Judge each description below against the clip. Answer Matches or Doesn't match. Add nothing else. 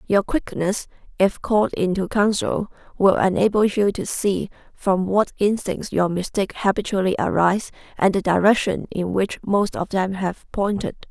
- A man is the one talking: Doesn't match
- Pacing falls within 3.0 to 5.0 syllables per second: Matches